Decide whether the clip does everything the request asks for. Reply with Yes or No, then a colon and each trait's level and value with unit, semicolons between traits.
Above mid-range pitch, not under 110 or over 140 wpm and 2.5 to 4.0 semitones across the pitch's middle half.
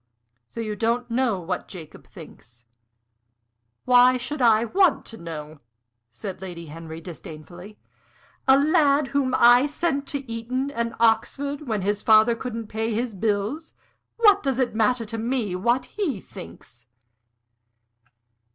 No: high, 230 Hz; slow, 135 wpm; average, 5.1 semitones